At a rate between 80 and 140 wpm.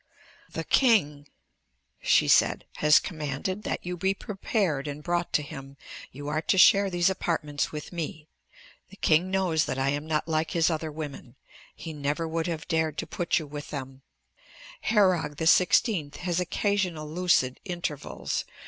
No: average, 155 wpm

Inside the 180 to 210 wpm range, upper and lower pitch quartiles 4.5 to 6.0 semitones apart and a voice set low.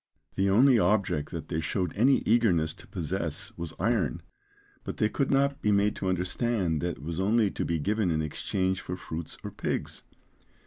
Yes: average, 185 wpm; average, 4.8 semitones; very low, 95 Hz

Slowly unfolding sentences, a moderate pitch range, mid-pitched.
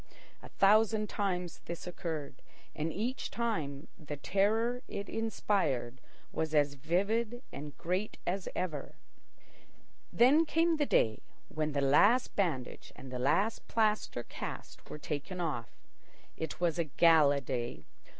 No: slow, 130 wpm; wide, 6.7 semitones; medium, 170 Hz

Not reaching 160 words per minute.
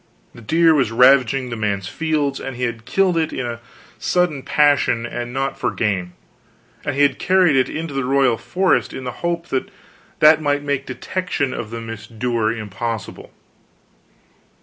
No: average, 165 wpm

